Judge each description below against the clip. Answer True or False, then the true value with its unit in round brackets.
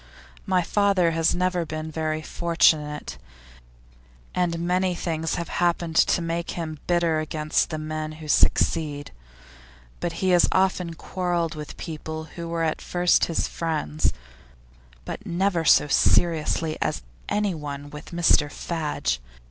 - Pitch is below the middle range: False (165 Hz)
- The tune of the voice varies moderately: False (2.0 semitones)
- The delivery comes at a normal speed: False (130 wpm)